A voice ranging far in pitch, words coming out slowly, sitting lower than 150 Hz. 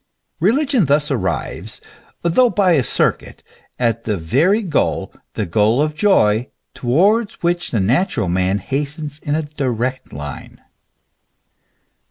Yes: wide, 8.0 semitones; slow, 125 wpm; medium, 140 Hz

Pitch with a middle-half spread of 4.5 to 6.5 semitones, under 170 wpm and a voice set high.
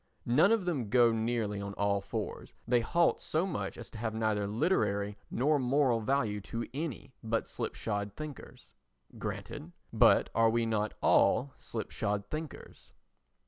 No: average, 4.9 semitones; average, 145 wpm; low, 115 Hz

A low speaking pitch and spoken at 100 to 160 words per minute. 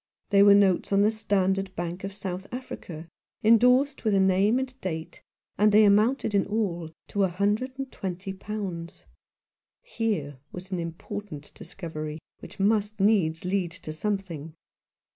No: high, 195 Hz; average, 150 wpm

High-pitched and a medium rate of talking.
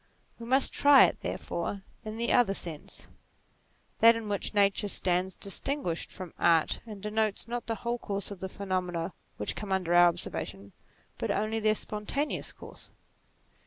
Yes: high, 200 Hz; average, 165 wpm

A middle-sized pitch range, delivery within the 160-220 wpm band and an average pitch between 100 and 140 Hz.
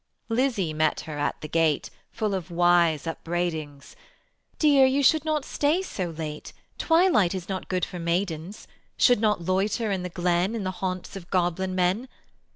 No: average, 4.4 semitones; average, 165 wpm; medium, 185 Hz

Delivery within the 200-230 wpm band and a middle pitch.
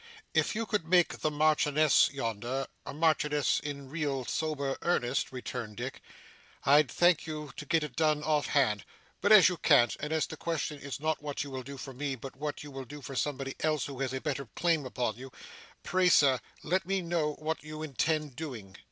Yes: fast, 205 wpm; medium, 145 Hz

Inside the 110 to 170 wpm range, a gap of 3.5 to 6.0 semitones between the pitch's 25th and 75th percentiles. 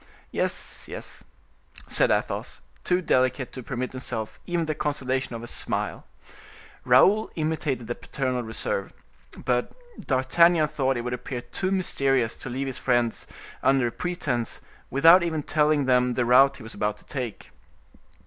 Yes: average, 150 wpm; average, 3.8 semitones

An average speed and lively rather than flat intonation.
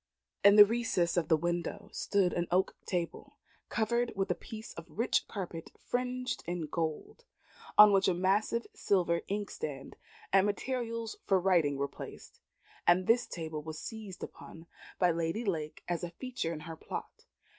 No: average, 160 wpm; average, 4.6 semitones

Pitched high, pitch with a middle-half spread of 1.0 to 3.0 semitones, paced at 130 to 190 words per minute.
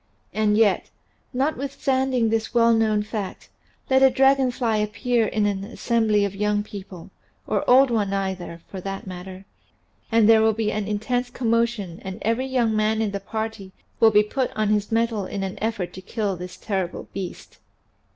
Yes: high, 215 Hz; average, 2.7 semitones; average, 175 wpm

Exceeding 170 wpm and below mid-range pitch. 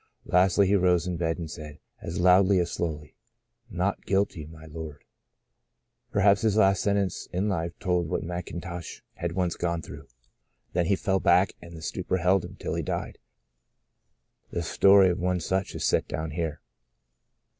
Yes: average, 180 wpm; very low, 90 Hz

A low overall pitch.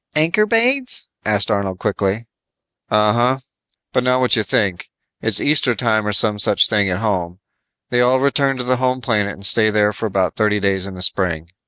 Yes: low, 105 Hz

